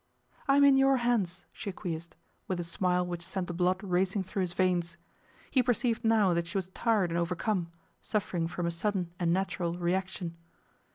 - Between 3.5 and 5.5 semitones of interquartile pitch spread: No, average, 3.1 semitones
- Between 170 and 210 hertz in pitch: Yes, medium, 185 Hz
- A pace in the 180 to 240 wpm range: Yes, average, 185 wpm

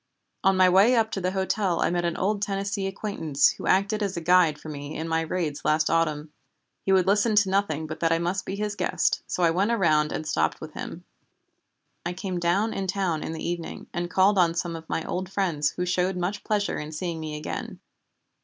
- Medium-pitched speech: Yes, medium, 180 Hz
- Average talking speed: No, fast, 225 wpm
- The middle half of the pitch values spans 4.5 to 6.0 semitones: No, average, 3.3 semitones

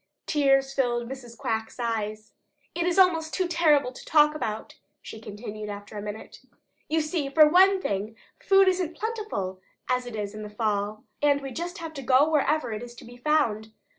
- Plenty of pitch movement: Yes, wide, 6.5 semitones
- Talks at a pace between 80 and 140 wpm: No, average, 195 wpm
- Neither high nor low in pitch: No, very high, 260 Hz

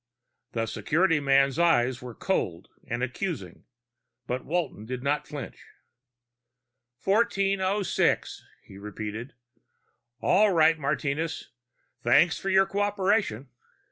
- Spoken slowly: Yes, slow, 100 wpm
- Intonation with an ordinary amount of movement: No, wide, 7.4 semitones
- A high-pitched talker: No, medium, 150 Hz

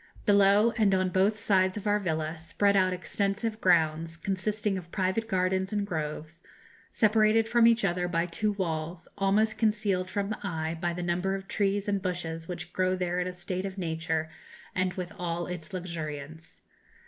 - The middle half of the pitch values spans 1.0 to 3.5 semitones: Yes, average, 3.0 semitones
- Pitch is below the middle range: No, medium, 185 Hz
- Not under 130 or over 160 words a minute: No, average, 175 wpm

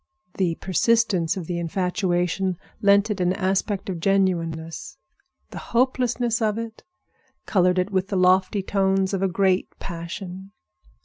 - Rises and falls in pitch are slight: Yes, narrow, 2.0 semitones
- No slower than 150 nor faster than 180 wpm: No, slow, 135 wpm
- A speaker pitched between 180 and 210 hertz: Yes, high, 190 Hz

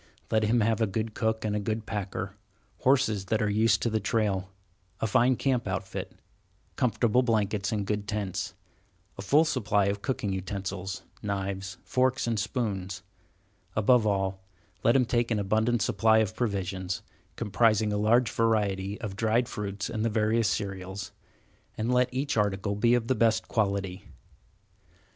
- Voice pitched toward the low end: Yes, low, 105 Hz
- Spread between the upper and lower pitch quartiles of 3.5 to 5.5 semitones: No, narrow, 2.5 semitones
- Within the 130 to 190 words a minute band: Yes, average, 155 wpm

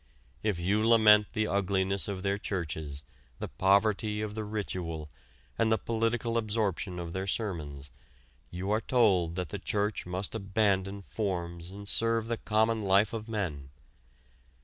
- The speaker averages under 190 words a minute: Yes, average, 150 wpm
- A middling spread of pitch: Yes, average, 3.2 semitones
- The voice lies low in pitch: Yes, low, 100 Hz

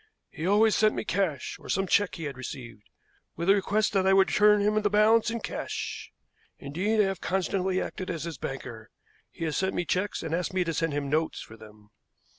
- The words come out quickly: Yes, fast, 220 wpm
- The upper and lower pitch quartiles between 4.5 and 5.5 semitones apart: Yes, average, 5.1 semitones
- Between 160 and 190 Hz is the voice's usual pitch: Yes, medium, 185 Hz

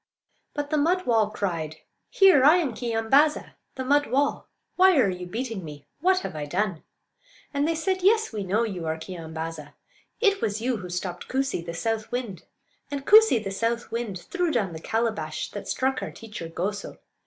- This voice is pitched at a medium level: No, high, 225 Hz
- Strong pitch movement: Yes, wide, 8.0 semitones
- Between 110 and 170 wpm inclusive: No, average, 185 wpm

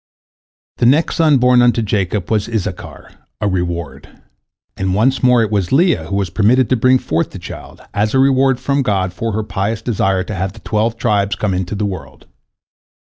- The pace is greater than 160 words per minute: Yes, average, 200 wpm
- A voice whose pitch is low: Yes, low, 105 Hz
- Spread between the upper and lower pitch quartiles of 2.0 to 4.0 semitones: No, average, 4.6 semitones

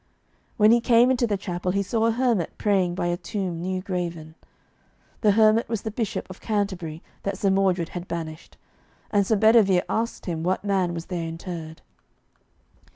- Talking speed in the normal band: Yes, average, 175 wpm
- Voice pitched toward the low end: No, high, 190 Hz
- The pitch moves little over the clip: No, average, 3.8 semitones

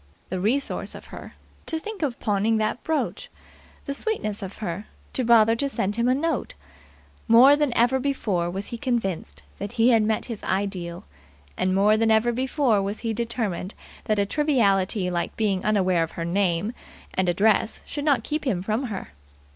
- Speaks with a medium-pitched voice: No, high, 220 Hz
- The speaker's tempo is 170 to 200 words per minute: Yes, average, 180 wpm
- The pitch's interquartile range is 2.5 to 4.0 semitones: No, average, 4.6 semitones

